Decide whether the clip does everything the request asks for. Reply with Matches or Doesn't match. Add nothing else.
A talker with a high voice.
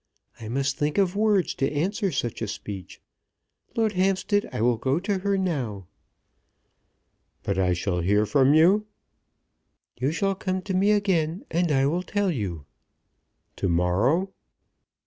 Doesn't match